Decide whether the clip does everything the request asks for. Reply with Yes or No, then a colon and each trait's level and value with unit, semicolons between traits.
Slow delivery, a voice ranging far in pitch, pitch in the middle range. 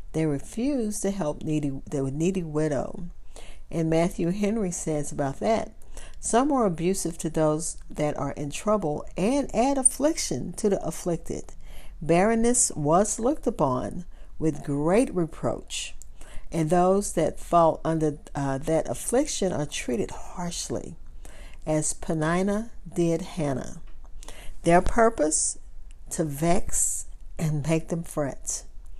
No: slow, 120 wpm; average, 4.8 semitones; medium, 165 Hz